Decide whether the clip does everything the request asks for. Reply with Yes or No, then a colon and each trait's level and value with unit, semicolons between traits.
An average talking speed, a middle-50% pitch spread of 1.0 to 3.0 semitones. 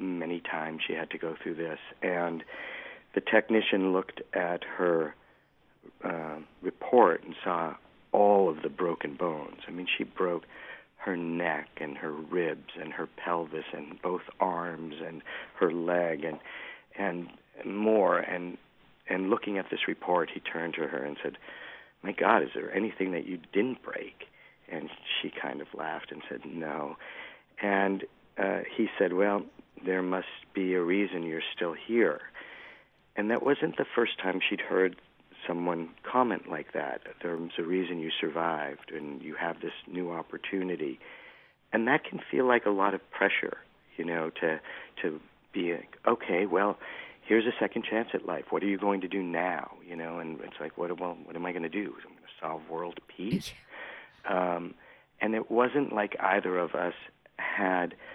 Yes: average, 170 wpm; average, 2.7 semitones